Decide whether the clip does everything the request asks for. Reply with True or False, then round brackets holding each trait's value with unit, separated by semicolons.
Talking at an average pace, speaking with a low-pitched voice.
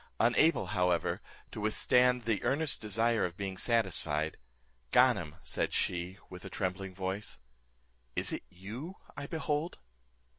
False (125 wpm; 100 Hz)